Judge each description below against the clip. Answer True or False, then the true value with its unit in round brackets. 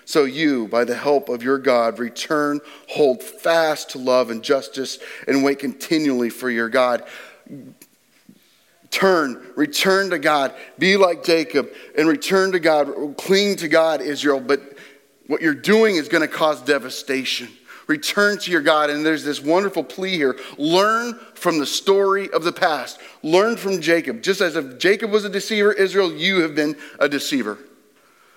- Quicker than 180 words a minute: False (165 wpm)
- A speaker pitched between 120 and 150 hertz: False (160 Hz)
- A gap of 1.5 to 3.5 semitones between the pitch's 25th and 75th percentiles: False (5.5 semitones)